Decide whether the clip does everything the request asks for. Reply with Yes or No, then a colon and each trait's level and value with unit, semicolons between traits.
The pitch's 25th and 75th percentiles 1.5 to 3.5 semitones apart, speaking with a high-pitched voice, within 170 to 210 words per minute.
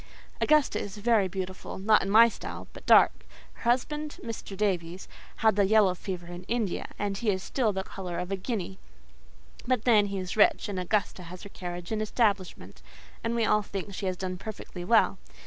Yes: average, 3.0 semitones; high, 200 Hz; average, 185 wpm